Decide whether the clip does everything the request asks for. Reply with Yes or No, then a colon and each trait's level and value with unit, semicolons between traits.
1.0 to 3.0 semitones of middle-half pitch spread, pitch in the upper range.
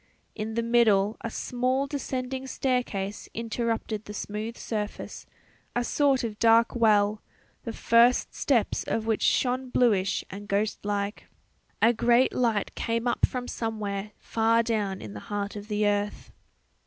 Yes: average, 2.7 semitones; high, 225 Hz